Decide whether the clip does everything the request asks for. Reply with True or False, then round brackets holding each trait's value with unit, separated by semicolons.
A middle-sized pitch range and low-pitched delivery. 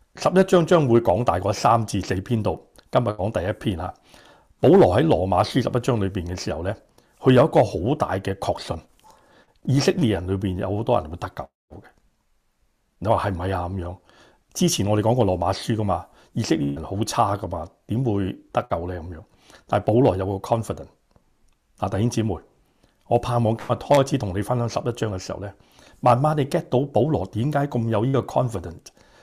True (4.4 semitones; 105 Hz)